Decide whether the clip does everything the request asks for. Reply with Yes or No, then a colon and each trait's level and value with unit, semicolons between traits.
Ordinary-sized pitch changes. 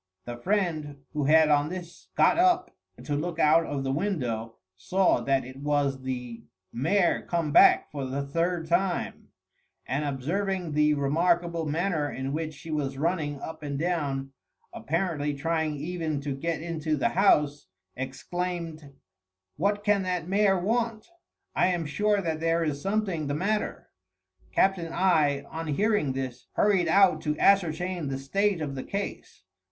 Yes: average, 4.1 semitones